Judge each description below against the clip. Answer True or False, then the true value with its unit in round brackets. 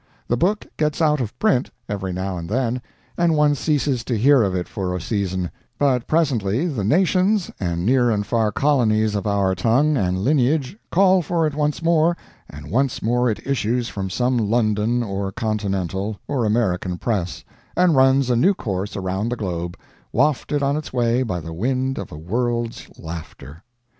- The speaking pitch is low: True (120 Hz)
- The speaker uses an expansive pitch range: True (6.4 semitones)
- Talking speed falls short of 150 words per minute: False (180 wpm)